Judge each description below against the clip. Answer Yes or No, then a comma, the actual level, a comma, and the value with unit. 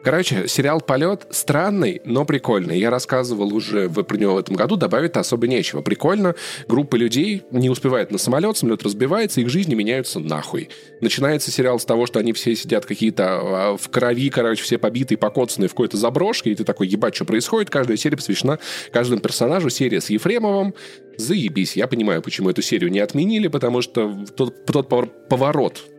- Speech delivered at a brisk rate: Yes, fast, 175 wpm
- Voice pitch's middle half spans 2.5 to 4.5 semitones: No, average, 5.0 semitones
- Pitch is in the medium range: No, low, 130 Hz